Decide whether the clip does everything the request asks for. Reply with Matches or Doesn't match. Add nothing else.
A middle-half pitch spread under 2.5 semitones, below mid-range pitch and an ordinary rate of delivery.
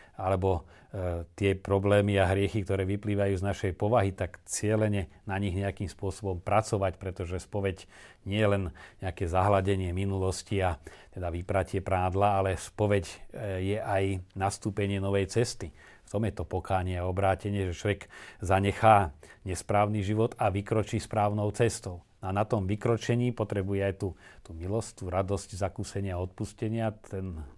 Matches